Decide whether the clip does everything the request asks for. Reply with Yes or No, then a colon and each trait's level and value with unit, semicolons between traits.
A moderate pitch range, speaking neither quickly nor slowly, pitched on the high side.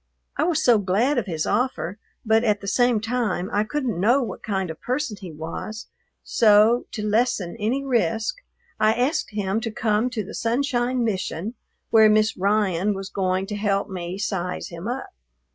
Yes: average, 3.8 semitones; average, 180 wpm; high, 215 Hz